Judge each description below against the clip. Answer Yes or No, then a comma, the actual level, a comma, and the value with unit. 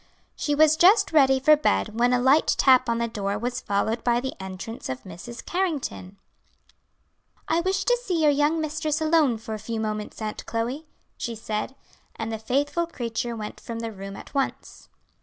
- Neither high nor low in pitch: No, high, 245 Hz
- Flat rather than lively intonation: No, wide, 5.6 semitones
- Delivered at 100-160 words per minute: No, average, 185 wpm